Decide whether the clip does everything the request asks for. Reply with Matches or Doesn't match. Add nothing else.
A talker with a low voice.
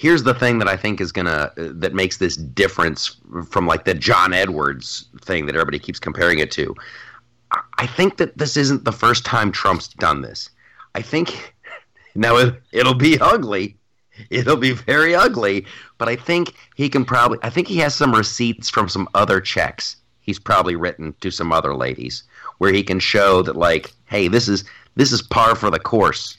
Matches